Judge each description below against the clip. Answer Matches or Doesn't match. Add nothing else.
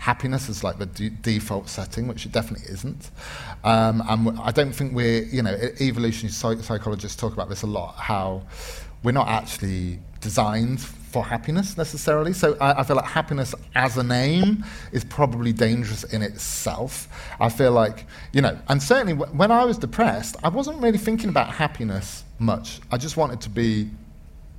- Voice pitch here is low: Matches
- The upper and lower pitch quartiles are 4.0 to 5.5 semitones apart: Matches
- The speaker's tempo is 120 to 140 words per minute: Doesn't match